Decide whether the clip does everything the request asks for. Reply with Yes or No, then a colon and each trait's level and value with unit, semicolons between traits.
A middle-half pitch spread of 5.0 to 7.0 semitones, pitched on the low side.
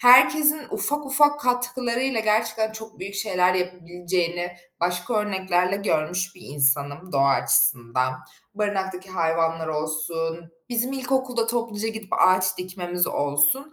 No: wide, 5.5 semitones; medium, 185 Hz